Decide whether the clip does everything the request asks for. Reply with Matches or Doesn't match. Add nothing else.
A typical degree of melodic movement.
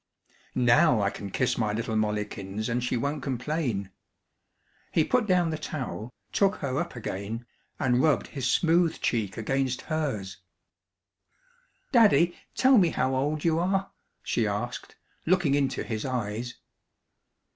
Doesn't match